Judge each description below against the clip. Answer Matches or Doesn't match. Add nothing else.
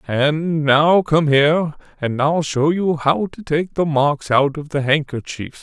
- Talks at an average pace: Matches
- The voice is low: Doesn't match